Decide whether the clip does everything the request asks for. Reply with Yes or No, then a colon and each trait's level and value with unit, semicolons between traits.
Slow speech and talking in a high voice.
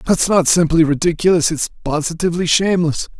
No: slow, 130 wpm; medium, 165 Hz